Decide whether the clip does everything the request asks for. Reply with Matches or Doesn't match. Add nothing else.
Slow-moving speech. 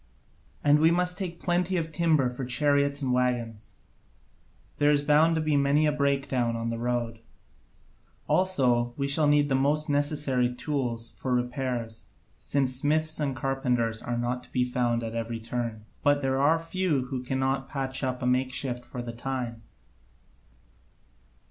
Doesn't match